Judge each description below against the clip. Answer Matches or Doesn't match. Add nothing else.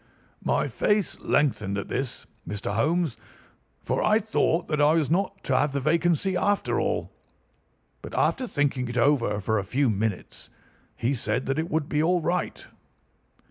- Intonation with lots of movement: Matches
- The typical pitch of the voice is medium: Matches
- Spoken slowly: Doesn't match